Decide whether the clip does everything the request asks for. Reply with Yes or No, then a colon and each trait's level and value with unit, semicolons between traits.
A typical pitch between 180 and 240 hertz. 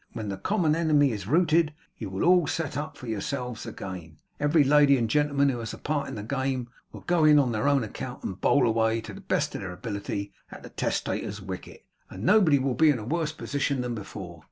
No: low, 130 Hz